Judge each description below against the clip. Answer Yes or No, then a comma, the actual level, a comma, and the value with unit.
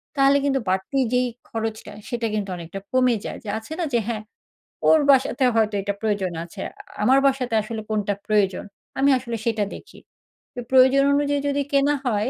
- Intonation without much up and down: No, average, 4.3 semitones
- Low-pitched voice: No, high, 235 Hz